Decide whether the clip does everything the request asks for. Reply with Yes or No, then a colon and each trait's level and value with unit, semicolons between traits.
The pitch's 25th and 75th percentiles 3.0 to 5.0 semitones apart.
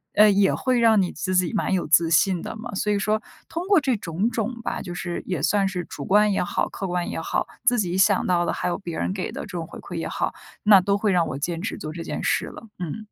Yes: average, 3.5 semitones